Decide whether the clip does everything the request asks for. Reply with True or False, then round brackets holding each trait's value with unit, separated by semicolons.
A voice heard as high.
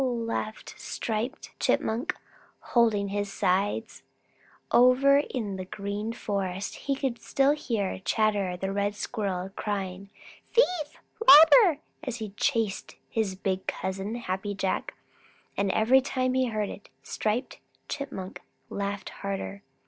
True (215 Hz)